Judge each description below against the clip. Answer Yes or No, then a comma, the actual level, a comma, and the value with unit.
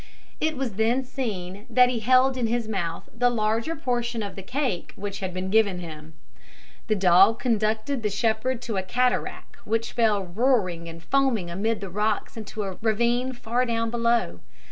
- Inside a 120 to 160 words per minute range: No, average, 170 wpm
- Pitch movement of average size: Yes, average, 3.9 semitones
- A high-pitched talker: Yes, high, 220 Hz